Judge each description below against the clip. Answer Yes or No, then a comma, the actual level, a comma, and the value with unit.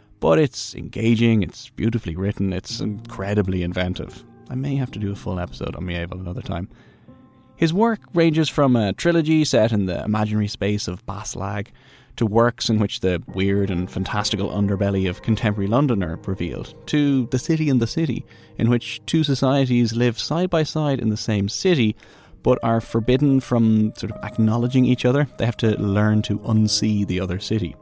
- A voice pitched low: Yes, low, 110 Hz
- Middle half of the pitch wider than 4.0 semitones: Yes, average, 4.4 semitones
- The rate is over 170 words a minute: Yes, average, 180 wpm